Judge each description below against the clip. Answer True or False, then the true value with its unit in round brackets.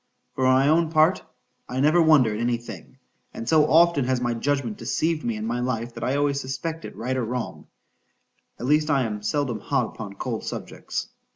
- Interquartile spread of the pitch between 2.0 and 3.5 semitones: False (4.3 semitones)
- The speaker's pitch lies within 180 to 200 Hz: False (130 Hz)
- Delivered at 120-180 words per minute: False (190 wpm)